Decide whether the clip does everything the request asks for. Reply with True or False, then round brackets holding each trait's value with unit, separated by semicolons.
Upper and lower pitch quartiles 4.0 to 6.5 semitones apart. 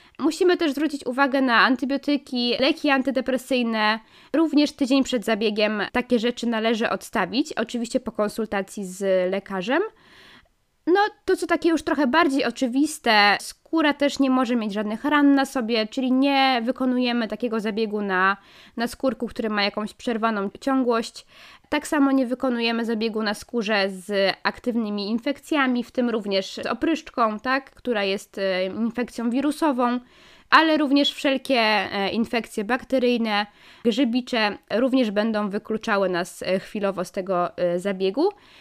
True (4.5 semitones)